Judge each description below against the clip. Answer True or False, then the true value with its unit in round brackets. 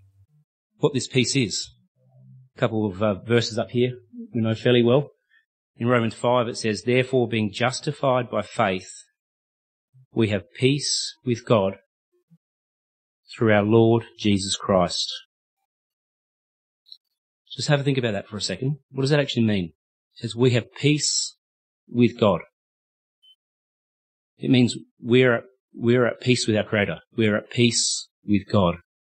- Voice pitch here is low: True (120 Hz)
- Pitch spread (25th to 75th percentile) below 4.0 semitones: True (3.5 semitones)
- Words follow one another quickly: False (145 wpm)